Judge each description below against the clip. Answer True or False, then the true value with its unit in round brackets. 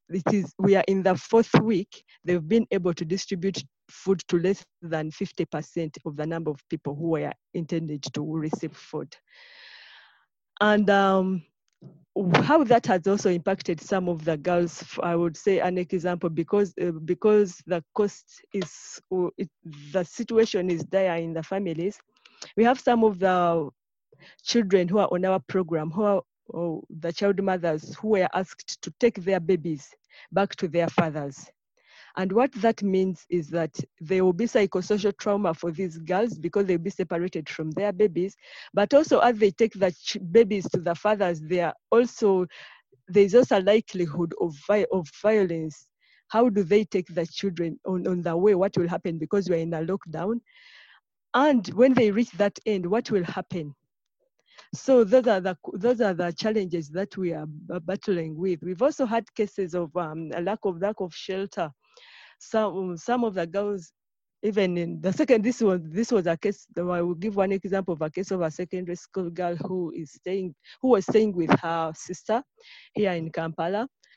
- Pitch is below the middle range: False (185 Hz)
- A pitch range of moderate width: True (3.4 semitones)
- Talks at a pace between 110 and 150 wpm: False (180 wpm)